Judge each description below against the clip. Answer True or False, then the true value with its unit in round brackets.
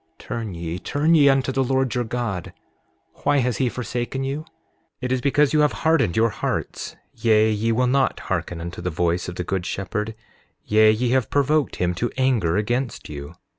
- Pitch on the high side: False (120 Hz)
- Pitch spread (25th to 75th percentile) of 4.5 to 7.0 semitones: True (5.5 semitones)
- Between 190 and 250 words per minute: True (195 wpm)